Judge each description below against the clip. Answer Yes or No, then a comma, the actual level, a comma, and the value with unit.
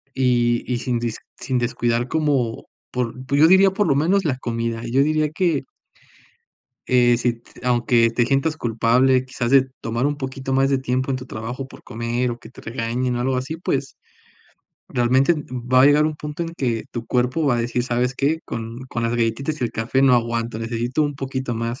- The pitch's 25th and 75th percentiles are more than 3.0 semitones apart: No, narrow, 2.6 semitones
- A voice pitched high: No, low, 125 Hz